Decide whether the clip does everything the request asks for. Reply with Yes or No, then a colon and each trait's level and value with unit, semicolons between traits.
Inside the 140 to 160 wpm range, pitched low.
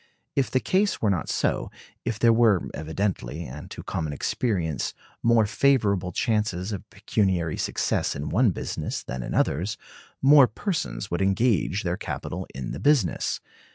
Yes: average, 155 wpm; low, 100 Hz